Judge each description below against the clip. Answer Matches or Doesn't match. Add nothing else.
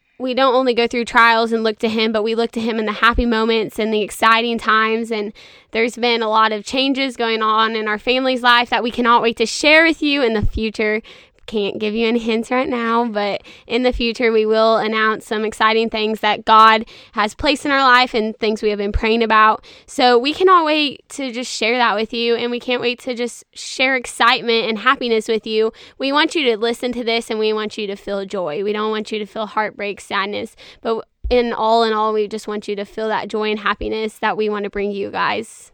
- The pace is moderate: Doesn't match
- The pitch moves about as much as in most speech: Doesn't match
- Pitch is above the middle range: Matches